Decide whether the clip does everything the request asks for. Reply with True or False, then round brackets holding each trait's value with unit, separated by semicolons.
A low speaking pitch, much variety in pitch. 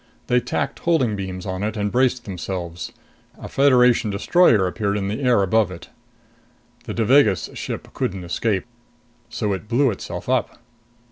False (105 Hz; 4.5 semitones)